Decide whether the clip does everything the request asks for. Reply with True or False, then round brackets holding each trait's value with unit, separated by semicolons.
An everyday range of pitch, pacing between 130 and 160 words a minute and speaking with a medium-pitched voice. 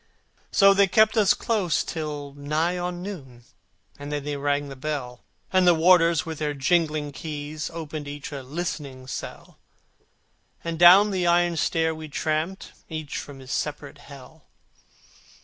True (3.4 semitones; 150 wpm; 155 Hz)